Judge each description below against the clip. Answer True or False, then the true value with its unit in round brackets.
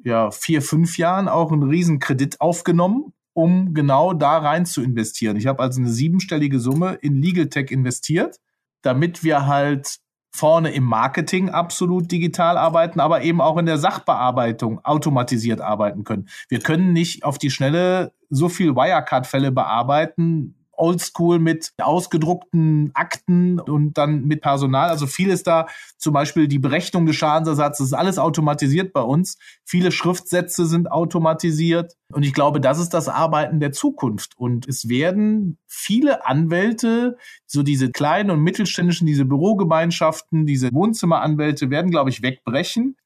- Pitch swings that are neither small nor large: True (3.7 semitones)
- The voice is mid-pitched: True (160 Hz)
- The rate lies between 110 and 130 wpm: False (150 wpm)